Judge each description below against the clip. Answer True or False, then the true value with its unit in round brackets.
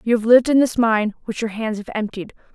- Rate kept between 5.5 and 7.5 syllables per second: True (6.2 syllables/s)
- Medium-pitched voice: False (225 Hz)